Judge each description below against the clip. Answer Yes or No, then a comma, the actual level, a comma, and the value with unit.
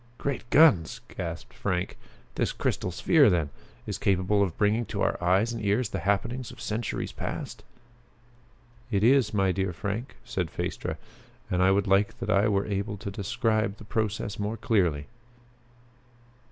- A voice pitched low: Yes, low, 100 Hz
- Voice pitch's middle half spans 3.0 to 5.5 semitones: No, narrow, 2.6 semitones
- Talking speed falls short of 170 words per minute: Yes, average, 155 wpm